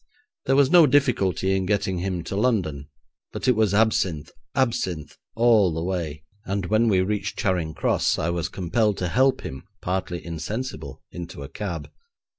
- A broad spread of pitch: No, average, 4.5 semitones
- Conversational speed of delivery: Yes, average, 165 wpm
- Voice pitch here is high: No, very low, 95 Hz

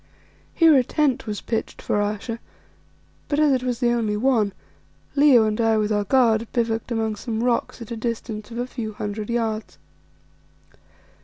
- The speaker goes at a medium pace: Yes, average, 170 wpm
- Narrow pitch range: Yes, narrow, 2.3 semitones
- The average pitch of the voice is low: No, high, 230 Hz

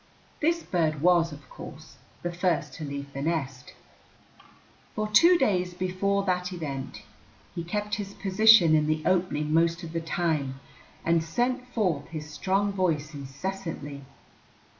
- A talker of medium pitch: Yes, medium, 170 Hz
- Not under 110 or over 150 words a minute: Yes, average, 140 wpm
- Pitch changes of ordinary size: Yes, average, 4.2 semitones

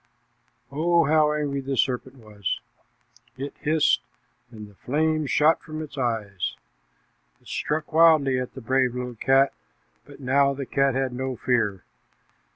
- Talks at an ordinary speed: Yes, average, 145 wpm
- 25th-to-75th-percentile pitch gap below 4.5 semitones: Yes, average, 3.3 semitones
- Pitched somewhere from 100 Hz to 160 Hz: Yes, low, 135 Hz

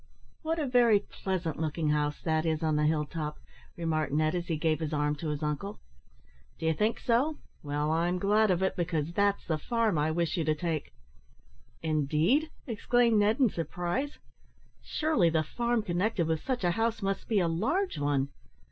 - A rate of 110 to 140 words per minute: No, average, 185 wpm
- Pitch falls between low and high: Yes, medium, 170 Hz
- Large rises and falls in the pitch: Yes, wide, 5.8 semitones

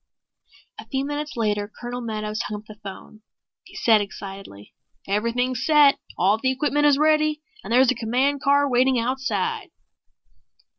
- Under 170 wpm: Yes, average, 150 wpm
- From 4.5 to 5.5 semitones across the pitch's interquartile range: Yes, average, 4.9 semitones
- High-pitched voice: Yes, very high, 250 Hz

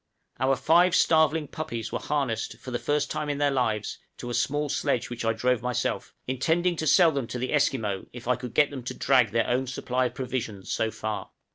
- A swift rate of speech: Yes, fast, 220 wpm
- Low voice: Yes, low, 130 Hz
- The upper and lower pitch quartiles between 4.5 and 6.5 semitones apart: No, average, 3.7 semitones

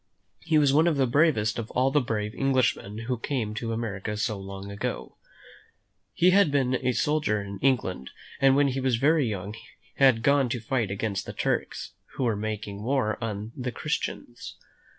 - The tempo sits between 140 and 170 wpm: No, average, 185 wpm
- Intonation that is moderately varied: Yes, average, 4.4 semitones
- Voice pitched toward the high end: No, low, 120 Hz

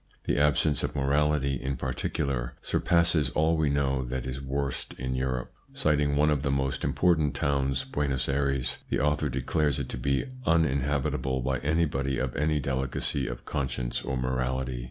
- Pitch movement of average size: No, narrow, 2.1 semitones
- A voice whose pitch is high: No, very low, 70 Hz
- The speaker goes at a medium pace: Yes, average, 160 wpm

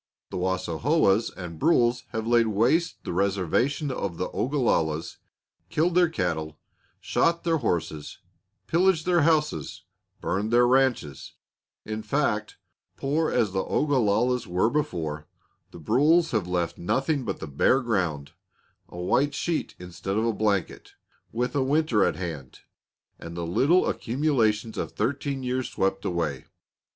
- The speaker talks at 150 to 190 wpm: No, average, 140 wpm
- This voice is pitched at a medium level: No, low, 115 Hz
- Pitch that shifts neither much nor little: No, wide, 7.8 semitones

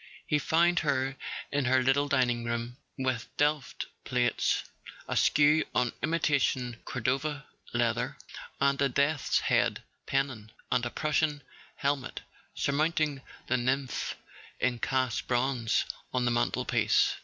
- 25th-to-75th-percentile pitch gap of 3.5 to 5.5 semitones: No, average, 2.8 semitones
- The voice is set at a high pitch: No, low, 135 Hz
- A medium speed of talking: No, slow, 120 wpm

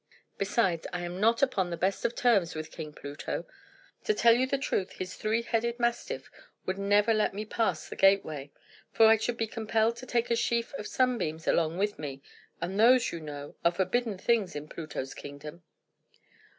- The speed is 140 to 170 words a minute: No, average, 190 wpm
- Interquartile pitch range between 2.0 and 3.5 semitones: No, wide, 5.6 semitones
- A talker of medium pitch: No, high, 200 Hz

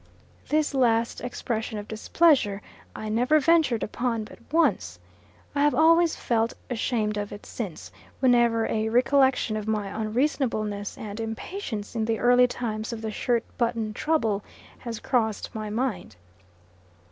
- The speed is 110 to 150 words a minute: Yes, average, 140 wpm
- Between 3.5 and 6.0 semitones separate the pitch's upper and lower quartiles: No, average, 2.9 semitones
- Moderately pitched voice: No, high, 230 Hz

